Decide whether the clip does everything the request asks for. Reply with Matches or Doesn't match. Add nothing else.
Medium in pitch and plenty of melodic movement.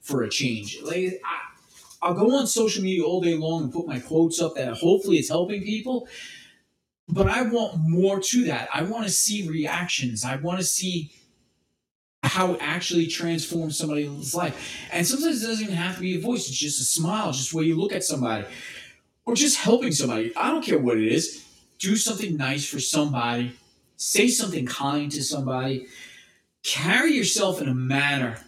Matches